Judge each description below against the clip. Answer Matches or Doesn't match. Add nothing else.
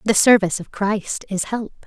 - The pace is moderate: Matches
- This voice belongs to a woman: Matches